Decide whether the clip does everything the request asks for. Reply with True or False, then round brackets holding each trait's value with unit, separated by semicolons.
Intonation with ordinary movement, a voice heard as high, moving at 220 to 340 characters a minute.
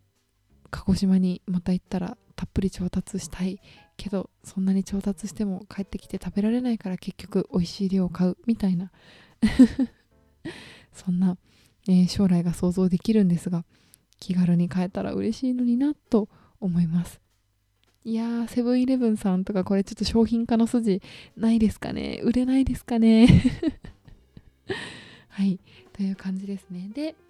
True (3.8 semitones; 195 Hz; 310 characters per minute)